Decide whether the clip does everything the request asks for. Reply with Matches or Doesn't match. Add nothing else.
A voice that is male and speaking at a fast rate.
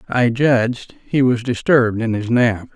Doesn't match